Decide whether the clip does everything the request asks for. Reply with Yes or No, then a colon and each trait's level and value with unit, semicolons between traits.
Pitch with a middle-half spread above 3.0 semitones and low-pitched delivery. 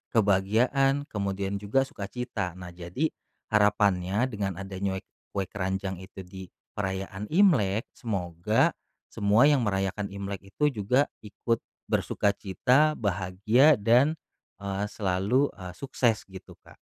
Yes: average, 4.0 semitones; low, 100 Hz